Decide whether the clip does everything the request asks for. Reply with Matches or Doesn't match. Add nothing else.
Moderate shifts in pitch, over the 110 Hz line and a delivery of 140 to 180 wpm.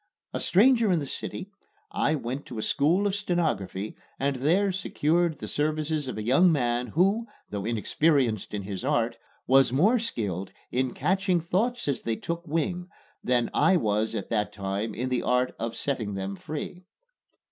Doesn't match